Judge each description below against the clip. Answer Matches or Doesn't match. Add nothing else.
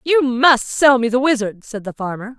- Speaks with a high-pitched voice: Matches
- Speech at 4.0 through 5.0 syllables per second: Matches